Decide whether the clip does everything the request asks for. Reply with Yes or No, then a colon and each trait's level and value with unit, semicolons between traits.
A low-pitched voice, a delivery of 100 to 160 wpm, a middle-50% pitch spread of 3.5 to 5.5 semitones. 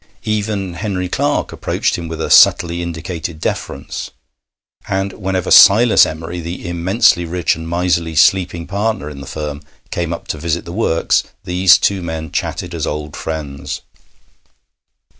No: very low, 85 Hz; average, 150 wpm; narrow, 2.5 semitones